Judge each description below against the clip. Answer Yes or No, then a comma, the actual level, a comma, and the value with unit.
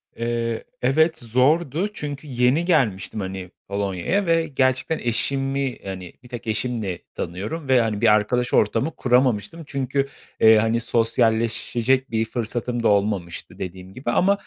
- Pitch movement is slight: No, average, 4.2 semitones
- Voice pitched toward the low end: Yes, low, 120 Hz